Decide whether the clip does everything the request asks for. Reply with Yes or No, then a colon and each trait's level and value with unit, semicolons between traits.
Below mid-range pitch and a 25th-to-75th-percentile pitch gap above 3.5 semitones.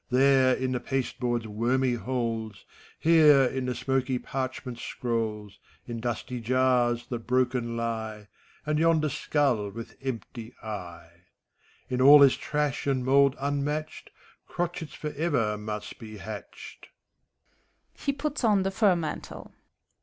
No: low, 125 Hz; average, 3.2 semitones